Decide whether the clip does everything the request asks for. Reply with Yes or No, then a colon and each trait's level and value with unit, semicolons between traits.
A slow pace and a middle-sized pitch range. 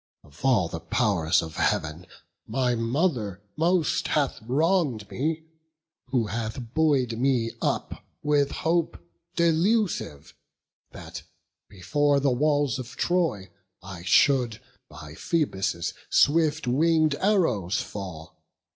No: slow, 110 wpm; wide, 7.7 semitones